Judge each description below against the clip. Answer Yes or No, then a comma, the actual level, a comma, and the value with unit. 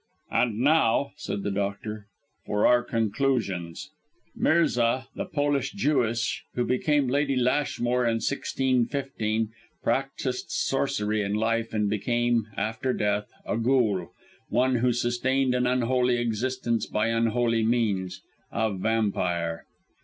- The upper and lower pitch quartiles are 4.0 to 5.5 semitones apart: No, average, 3.2 semitones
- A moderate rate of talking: No, slow, 115 wpm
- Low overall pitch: Yes, low, 120 Hz